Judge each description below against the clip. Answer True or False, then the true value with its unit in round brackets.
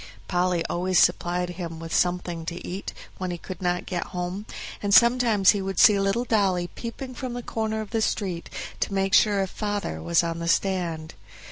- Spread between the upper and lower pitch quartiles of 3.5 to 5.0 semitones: False (3.0 semitones)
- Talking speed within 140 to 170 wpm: False (195 wpm)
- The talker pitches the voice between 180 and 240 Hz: True (185 Hz)